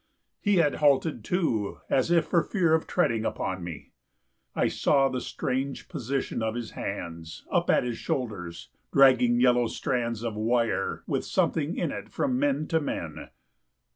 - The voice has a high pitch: No, low, 125 Hz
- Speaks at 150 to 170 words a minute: Yes, average, 160 wpm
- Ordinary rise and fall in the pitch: No, wide, 5.7 semitones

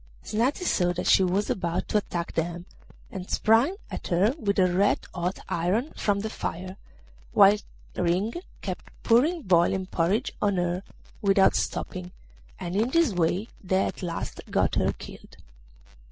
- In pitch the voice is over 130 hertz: Yes, high, 190 Hz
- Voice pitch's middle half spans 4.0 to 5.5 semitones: No, average, 3.3 semitones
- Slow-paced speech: No, average, 155 wpm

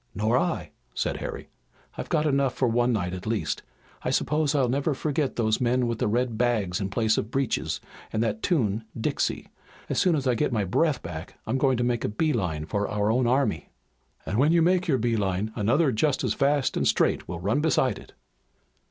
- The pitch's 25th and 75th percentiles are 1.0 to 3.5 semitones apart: No, average, 4.7 semitones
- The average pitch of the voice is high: No, low, 120 Hz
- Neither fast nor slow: No, fast, 215 wpm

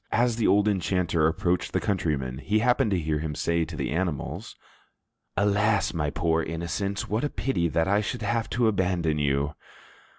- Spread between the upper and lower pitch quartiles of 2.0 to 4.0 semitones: No, average, 4.4 semitones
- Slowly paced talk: No, average, 175 wpm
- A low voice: Yes, very low, 90 Hz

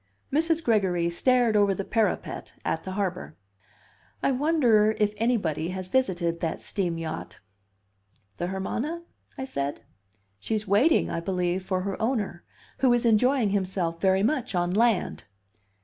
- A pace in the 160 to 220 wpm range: No, average, 140 wpm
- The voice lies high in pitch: Yes, high, 200 Hz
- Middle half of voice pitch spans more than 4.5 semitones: Yes, average, 5.0 semitones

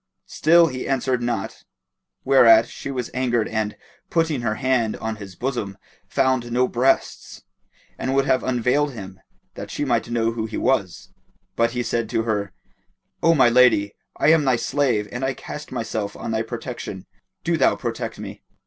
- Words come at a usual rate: Yes, average, 170 wpm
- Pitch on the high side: No, low, 120 Hz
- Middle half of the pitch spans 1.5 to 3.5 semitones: Yes, average, 2.9 semitones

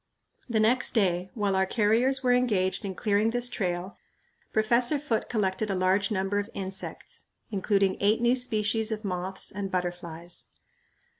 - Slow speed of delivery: No, average, 150 wpm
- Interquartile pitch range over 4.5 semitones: No, average, 3.1 semitones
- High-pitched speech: Yes, high, 205 Hz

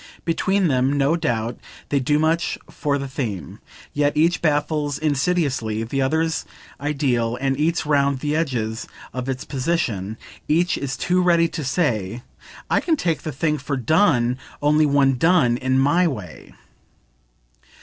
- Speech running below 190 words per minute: Yes, average, 150 wpm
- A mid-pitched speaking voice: Yes, medium, 145 Hz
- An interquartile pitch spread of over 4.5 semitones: No, average, 4.0 semitones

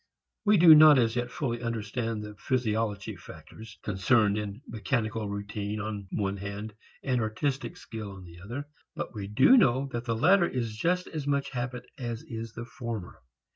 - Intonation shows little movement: No, average, 3.5 semitones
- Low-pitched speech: Yes, low, 115 Hz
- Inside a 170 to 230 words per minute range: Yes, average, 175 wpm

